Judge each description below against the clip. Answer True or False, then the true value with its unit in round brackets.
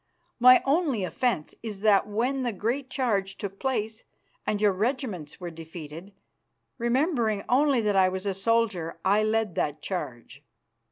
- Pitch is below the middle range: False (210 Hz)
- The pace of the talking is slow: False (150 wpm)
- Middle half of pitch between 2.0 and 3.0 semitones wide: False (4.5 semitones)